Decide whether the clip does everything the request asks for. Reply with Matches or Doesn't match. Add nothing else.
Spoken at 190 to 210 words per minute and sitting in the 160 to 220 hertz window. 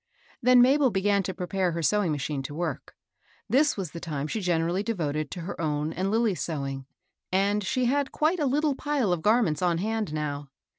Matches